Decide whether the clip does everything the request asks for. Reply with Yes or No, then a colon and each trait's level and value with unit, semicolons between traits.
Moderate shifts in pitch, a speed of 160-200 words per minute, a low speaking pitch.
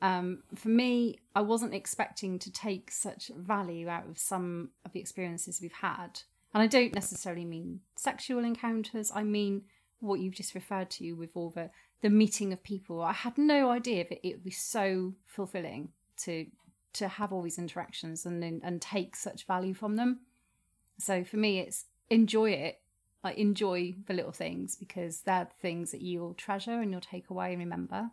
No: average, 3.3 semitones; average, 190 wpm; high, 190 Hz